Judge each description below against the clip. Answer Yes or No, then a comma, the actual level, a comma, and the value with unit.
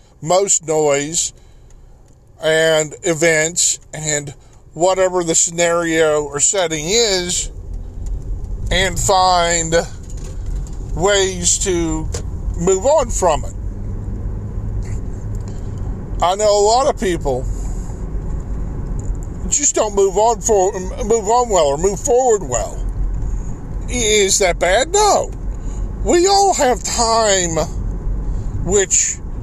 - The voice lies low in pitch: No, medium, 155 Hz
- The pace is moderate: No, slow, 95 wpm